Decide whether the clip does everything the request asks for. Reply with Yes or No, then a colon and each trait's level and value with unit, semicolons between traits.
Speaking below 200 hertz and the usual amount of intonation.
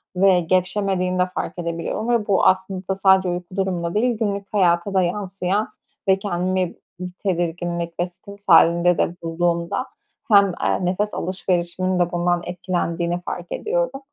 No: medium, 185 Hz; narrow, 2.0 semitones